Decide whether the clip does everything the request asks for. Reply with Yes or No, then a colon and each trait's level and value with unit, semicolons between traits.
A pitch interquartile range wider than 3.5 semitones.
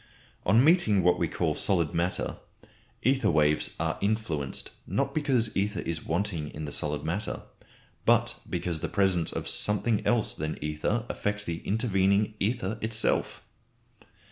Yes: average, 4.9 semitones